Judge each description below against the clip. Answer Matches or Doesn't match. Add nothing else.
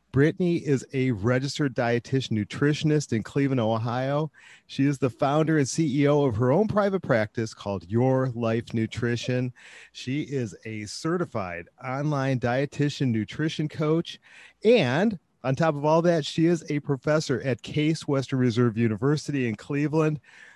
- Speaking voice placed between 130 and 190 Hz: Matches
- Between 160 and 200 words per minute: Doesn't match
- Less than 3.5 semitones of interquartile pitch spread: Doesn't match